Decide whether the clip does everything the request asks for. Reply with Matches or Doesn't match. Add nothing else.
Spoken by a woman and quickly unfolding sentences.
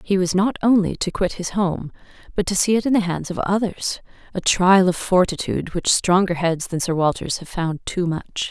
Matches